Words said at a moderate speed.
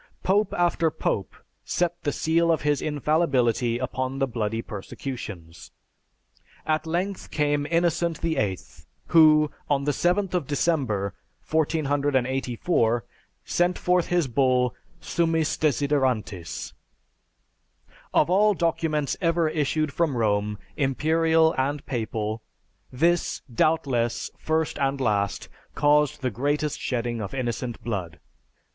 No: slow, 110 wpm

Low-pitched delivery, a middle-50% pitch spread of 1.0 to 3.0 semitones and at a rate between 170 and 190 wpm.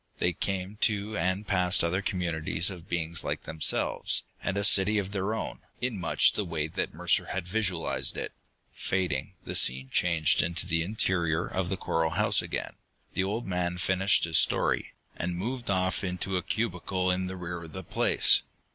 Yes: very low, 90 Hz; narrow, 2.4 semitones; average, 180 wpm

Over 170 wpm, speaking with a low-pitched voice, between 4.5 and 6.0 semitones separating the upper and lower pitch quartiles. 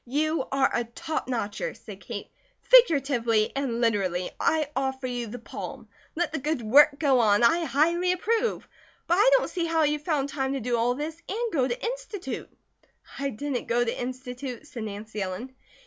No: average, 180 wpm; very high, 270 Hz; average, 5.2 semitones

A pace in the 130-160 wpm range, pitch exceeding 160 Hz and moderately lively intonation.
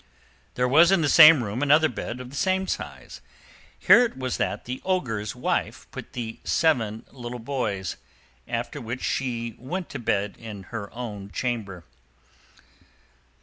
No: average, 150 wpm; low, 125 Hz; average, 4.6 semitones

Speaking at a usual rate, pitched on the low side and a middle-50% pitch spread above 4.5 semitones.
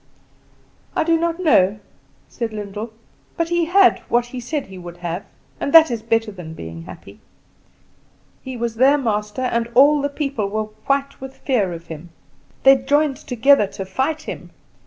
No: average, 170 wpm; high, 240 Hz; wide, 5.5 semitones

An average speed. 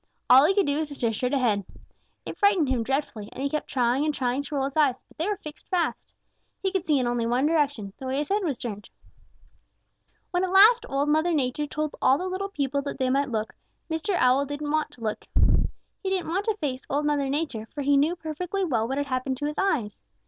No: fast, 240 wpm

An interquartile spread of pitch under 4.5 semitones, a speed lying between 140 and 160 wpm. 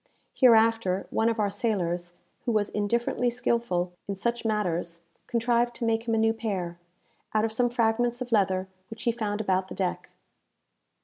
No: average, 3.6 semitones; average, 170 wpm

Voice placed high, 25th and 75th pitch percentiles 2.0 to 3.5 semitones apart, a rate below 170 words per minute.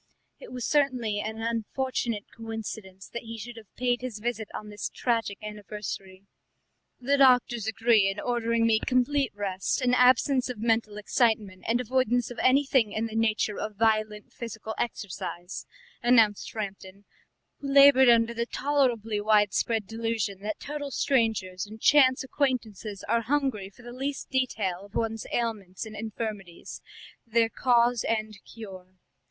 Yes: high, 225 Hz; average, 2.8 semitones; average, 145 wpm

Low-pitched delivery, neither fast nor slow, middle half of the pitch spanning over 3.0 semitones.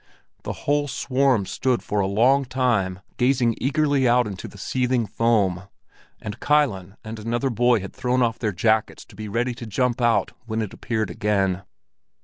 Yes: low, 115 Hz; average, 170 wpm; average, 3.5 semitones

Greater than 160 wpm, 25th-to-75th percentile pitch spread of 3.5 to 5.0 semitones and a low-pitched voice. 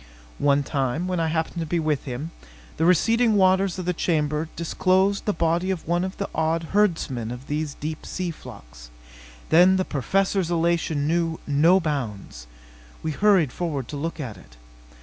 No: average, 170 wpm; average, 4.1 semitones; medium, 165 Hz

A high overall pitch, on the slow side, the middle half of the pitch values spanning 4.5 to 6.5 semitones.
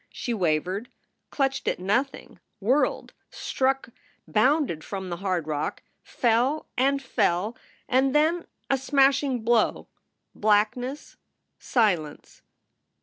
Yes: high, 240 Hz; slow, 100 wpm; wide, 5.5 semitones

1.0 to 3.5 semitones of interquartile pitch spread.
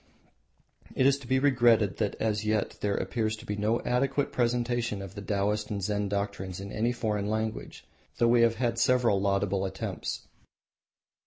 Yes: average, 2.9 semitones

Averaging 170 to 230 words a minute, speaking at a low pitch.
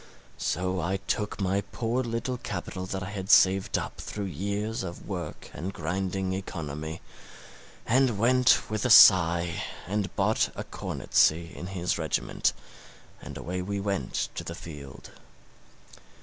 No: average, 140 wpm; very low, 95 Hz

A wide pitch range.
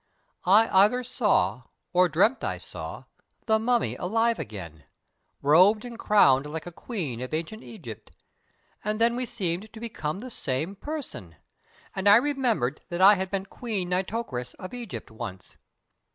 Yes: wide, 7.3 semitones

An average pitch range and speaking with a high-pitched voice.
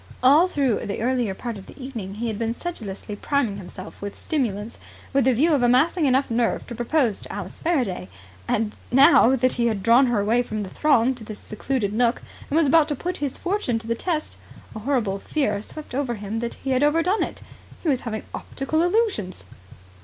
Yes: average, 4.9 semitones; high, 245 Hz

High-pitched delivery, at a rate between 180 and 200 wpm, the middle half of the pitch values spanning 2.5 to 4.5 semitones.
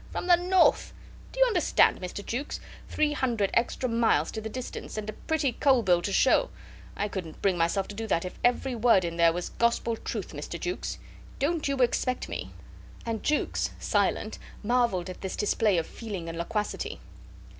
No: high, 225 Hz; average, 190 wpm; wide, 5.6 semitones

